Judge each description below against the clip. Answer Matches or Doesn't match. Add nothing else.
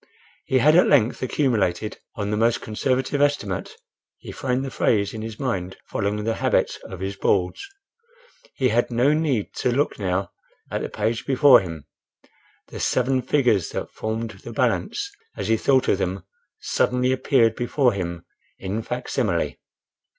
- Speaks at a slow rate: Doesn't match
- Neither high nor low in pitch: Doesn't match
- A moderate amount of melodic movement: Matches